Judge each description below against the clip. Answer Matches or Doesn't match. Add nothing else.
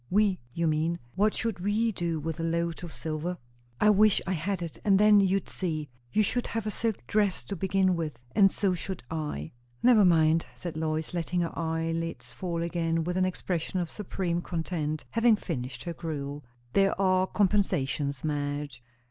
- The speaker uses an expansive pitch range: Doesn't match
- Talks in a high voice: Doesn't match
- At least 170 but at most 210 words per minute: Matches